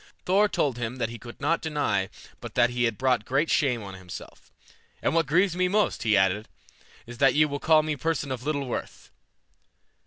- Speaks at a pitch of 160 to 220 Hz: No, low, 135 Hz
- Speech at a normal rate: No, fast, 210 wpm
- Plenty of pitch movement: No, average, 5.0 semitones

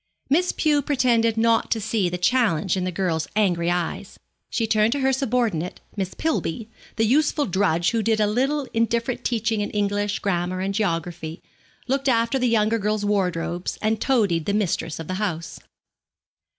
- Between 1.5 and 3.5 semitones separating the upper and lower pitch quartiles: No, average, 4.4 semitones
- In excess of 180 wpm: No, average, 170 wpm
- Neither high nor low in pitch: No, high, 210 Hz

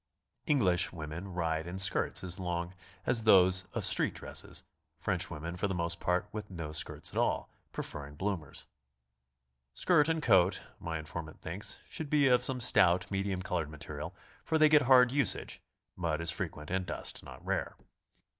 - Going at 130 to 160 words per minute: No, average, 175 wpm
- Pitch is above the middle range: No, very low, 90 Hz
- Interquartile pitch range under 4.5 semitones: No, average, 4.8 semitones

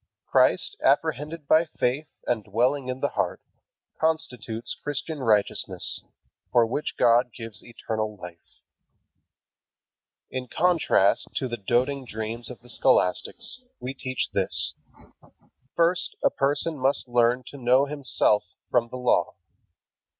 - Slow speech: Yes, slow, 120 wpm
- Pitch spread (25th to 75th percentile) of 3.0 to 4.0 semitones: Yes, average, 3.7 semitones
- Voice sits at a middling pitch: No, low, 125 Hz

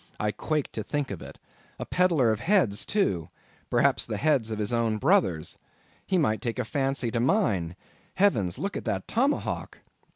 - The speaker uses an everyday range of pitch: No, wide, 8.6 semitones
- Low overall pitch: Yes, low, 125 Hz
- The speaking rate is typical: Yes, average, 165 wpm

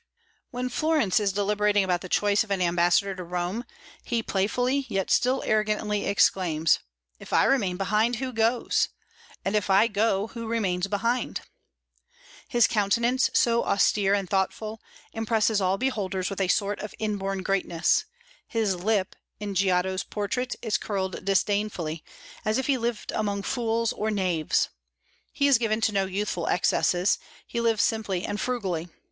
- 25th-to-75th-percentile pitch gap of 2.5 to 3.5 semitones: Yes, average, 3.0 semitones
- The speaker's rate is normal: Yes, average, 155 wpm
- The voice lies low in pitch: No, high, 205 Hz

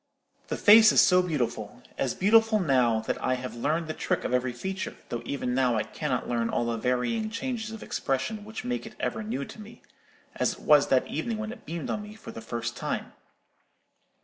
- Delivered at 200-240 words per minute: Yes, fast, 205 wpm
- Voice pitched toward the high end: No, medium, 160 Hz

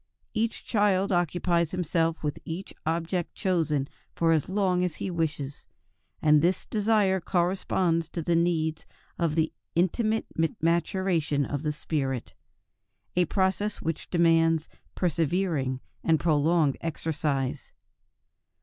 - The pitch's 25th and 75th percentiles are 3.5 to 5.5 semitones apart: No, average, 2.9 semitones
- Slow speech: Yes, slow, 115 wpm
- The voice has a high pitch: No, medium, 165 Hz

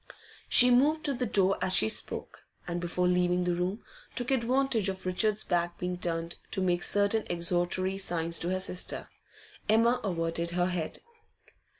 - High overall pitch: No, medium, 180 Hz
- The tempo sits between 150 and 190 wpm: Yes, average, 165 wpm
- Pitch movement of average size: Yes, average, 3.7 semitones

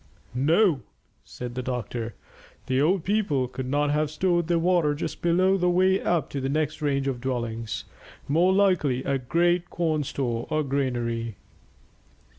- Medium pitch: Yes, medium, 145 Hz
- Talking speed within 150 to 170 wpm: Yes, average, 155 wpm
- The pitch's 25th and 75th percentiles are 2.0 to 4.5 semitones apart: No, average, 5.3 semitones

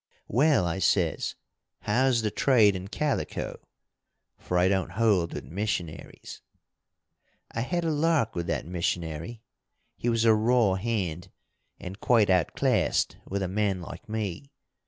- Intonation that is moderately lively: Yes, average, 4.4 semitones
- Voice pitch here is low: Yes, low, 105 Hz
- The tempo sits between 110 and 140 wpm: Yes, slow, 135 wpm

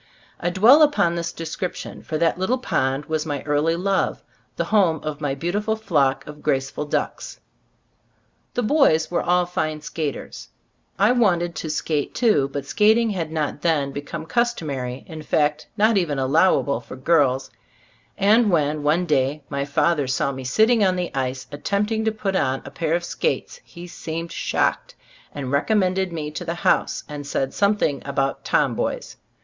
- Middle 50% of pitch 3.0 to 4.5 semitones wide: No, average, 5.0 semitones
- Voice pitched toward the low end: No, medium, 160 Hz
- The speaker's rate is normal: Yes, average, 165 wpm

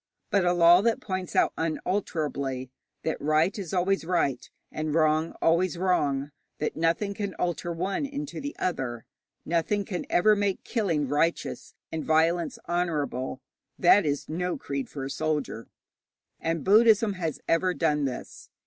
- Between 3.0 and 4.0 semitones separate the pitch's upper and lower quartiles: Yes, average, 3.6 semitones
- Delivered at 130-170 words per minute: Yes, average, 150 wpm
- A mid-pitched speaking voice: Yes, medium, 170 Hz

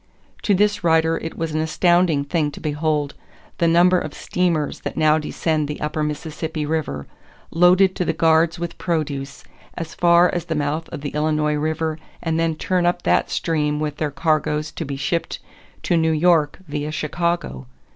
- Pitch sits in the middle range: Yes, medium, 160 Hz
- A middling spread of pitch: No, narrow, 2.1 semitones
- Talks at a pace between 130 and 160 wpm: No, average, 175 wpm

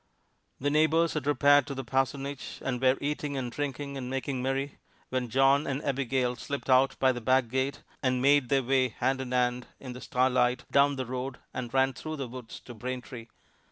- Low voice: Yes, low, 130 Hz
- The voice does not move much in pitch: Yes, narrow, 1.8 semitones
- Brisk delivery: No, average, 195 wpm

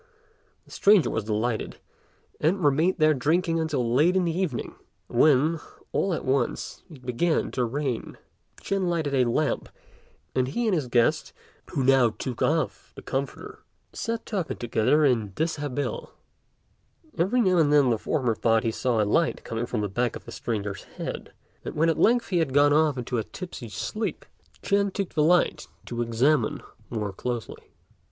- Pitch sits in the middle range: Yes, medium, 145 Hz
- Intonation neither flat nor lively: No, wide, 5.7 semitones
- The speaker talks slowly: No, average, 170 wpm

